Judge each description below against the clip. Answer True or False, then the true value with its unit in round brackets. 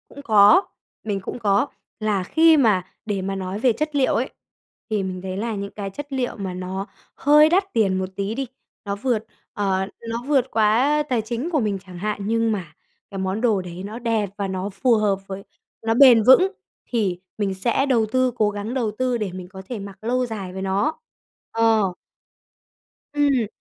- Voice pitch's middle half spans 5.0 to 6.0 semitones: False (4.3 semitones)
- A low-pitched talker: False (215 Hz)